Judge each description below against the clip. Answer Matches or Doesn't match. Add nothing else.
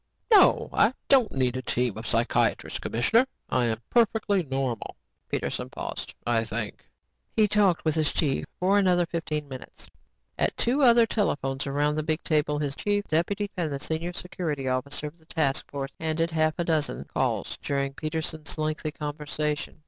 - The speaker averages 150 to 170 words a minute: Matches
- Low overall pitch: Doesn't match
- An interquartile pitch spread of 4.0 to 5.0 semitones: Matches